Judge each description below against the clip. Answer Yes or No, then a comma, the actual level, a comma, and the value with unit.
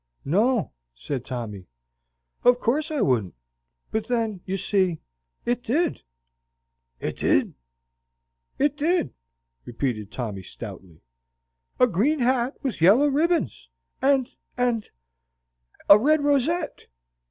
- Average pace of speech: No, slow, 105 wpm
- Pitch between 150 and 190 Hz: No, high, 235 Hz